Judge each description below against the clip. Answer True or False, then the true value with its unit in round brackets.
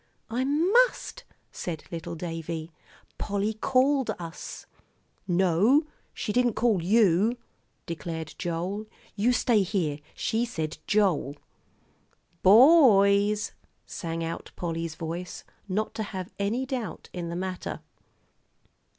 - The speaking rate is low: True (110 wpm)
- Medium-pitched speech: False (200 Hz)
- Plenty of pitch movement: True (5.7 semitones)